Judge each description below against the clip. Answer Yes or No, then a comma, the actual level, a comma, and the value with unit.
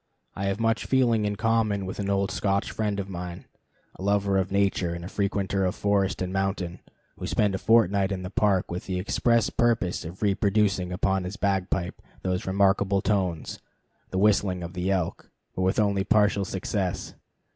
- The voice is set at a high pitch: No, very low, 95 Hz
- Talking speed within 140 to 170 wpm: No, average, 180 wpm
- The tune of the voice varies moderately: No, narrow, 1.8 semitones